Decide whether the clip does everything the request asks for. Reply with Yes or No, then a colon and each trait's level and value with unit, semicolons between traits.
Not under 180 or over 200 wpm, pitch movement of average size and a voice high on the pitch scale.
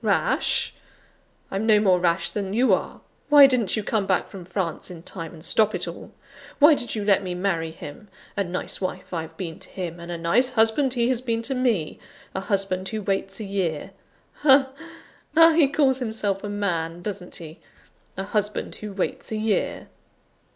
Yes: average, 190 wpm; average, 4.2 semitones; high, 200 Hz